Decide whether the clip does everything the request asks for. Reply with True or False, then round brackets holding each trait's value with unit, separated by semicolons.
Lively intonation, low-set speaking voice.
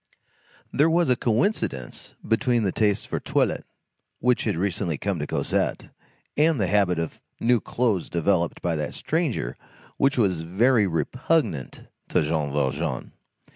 True (7.1 semitones; 100 Hz)